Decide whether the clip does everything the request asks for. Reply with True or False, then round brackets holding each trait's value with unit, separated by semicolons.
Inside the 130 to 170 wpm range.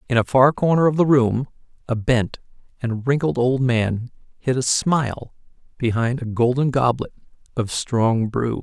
True (160 wpm)